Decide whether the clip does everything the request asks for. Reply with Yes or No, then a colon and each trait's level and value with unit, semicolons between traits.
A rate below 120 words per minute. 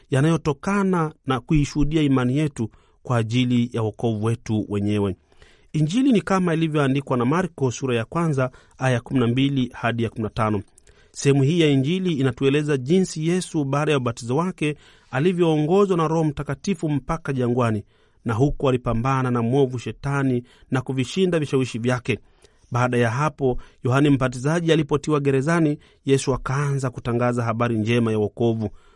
No: average, 125 wpm